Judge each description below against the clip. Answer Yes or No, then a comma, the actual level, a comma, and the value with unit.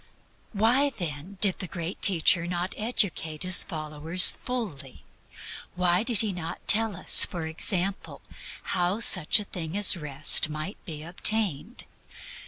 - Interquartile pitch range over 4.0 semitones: Yes, average, 4.4 semitones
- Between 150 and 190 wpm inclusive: No, slow, 135 wpm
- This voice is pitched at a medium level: Yes, medium, 180 Hz